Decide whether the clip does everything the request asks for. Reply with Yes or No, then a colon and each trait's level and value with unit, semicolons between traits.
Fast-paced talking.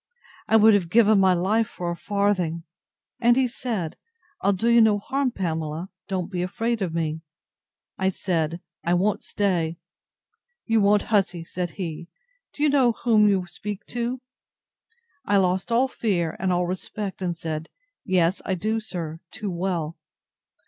No: average, 160 wpm